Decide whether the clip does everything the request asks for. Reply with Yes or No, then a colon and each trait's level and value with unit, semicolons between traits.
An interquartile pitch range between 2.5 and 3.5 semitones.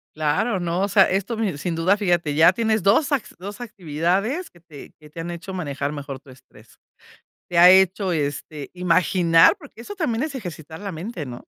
No: average, 4.5 semitones